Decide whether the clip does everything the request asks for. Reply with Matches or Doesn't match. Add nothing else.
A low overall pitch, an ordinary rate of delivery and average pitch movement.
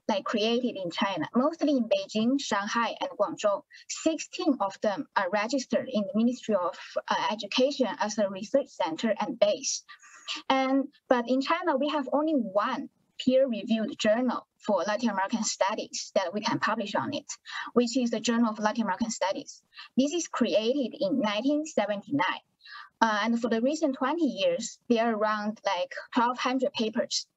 Doesn't match